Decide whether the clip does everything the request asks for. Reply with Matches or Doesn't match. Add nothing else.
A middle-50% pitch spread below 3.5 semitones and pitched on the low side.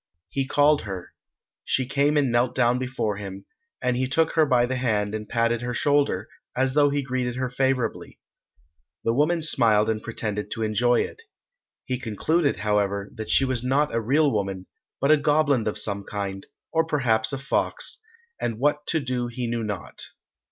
Doesn't match